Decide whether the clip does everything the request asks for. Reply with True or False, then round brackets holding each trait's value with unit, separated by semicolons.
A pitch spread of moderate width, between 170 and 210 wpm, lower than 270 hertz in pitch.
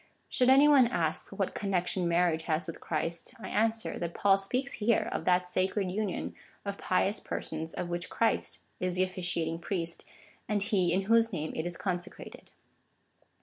True (3.4 semitones; 175 wpm; 185 Hz)